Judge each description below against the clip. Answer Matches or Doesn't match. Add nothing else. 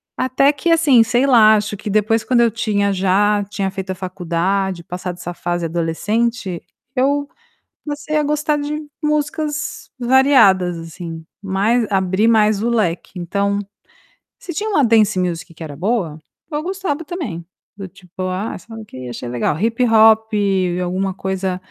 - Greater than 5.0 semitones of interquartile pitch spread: Matches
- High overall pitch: Matches